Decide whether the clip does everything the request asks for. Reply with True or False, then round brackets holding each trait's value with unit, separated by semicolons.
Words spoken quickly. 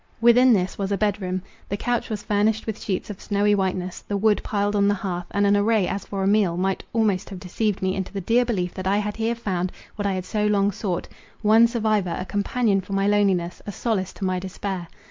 True (235 wpm)